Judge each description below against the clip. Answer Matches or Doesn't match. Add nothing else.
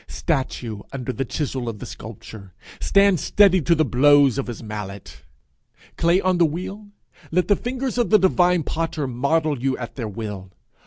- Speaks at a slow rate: Doesn't match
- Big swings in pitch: Matches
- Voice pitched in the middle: Matches